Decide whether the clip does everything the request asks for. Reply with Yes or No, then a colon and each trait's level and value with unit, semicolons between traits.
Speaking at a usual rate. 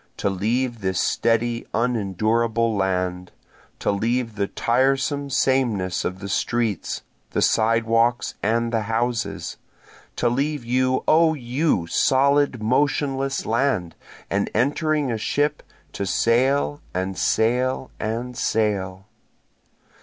No: slow, 110 wpm